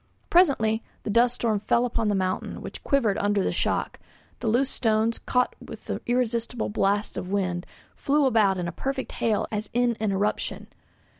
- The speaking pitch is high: Yes, high, 220 Hz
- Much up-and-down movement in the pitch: No, average, 3.2 semitones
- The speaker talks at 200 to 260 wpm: No, average, 175 wpm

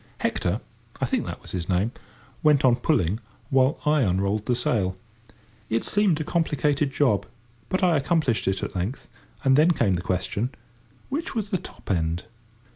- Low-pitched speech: Yes, low, 130 Hz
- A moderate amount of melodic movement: No, wide, 7.7 semitones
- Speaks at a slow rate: No, average, 160 wpm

